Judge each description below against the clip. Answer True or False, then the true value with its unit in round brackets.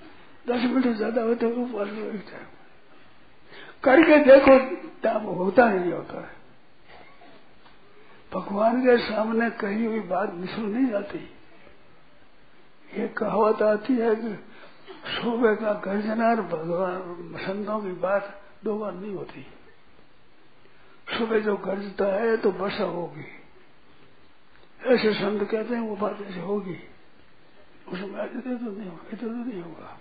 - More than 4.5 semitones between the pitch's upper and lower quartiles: False (2.7 semitones)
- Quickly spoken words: False (120 wpm)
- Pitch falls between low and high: False (215 Hz)